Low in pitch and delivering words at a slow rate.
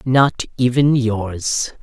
Yes: low, 120 Hz; slow, 100 wpm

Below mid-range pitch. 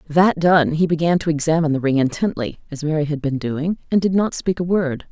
No: medium, 160 Hz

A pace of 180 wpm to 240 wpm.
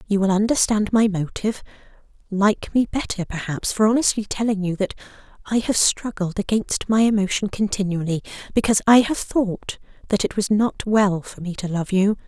No: average, 165 wpm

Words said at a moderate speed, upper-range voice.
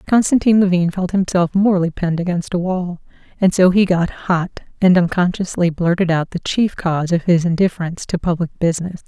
No: average, 180 wpm; medium, 180 Hz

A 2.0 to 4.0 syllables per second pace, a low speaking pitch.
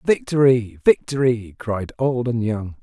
Yes: 3.9 syllables/s; low, 120 Hz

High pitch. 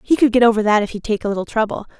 Yes: high, 220 Hz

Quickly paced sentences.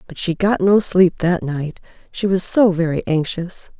No: average, 190 wpm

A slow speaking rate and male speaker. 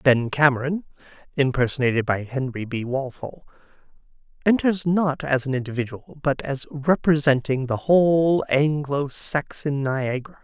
Yes: slow, 115 wpm; male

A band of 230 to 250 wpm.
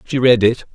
Yes: fast, 245 wpm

